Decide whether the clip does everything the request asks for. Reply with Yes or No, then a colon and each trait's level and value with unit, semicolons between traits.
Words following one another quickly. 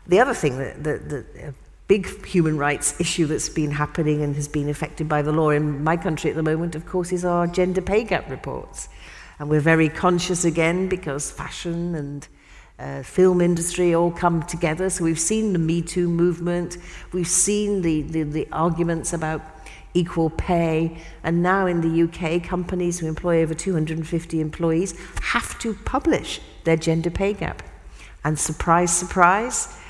No: average, 175 wpm